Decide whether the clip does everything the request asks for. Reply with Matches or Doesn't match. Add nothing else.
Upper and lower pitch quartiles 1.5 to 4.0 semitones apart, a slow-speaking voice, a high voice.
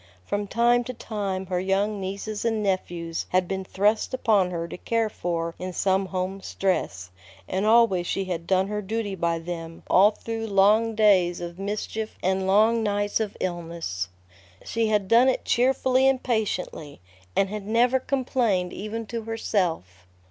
Doesn't match